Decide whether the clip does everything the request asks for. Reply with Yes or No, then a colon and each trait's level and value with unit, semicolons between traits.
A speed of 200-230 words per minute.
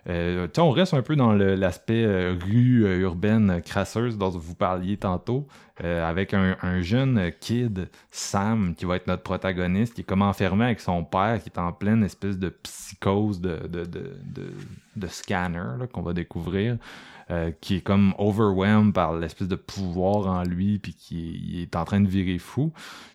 No: average, 185 wpm